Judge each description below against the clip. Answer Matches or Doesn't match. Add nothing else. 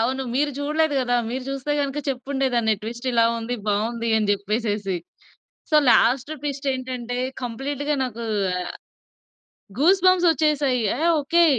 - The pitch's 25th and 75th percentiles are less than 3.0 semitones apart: Doesn't match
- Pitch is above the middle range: Matches